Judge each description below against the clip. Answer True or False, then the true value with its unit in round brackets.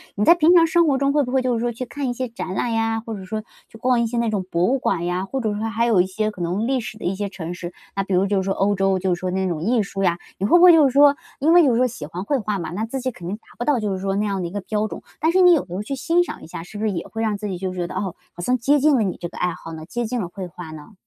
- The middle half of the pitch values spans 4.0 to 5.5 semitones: True (5.2 semitones)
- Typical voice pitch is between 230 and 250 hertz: False (215 Hz)